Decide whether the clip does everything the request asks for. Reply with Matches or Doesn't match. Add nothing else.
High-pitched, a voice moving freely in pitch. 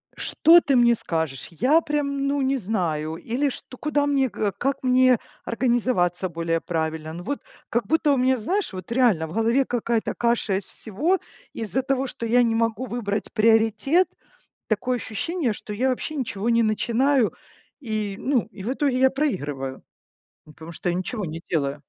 Matches